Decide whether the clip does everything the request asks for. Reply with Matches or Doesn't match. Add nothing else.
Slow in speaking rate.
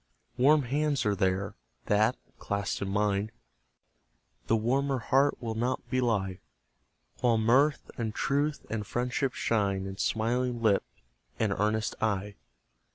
Matches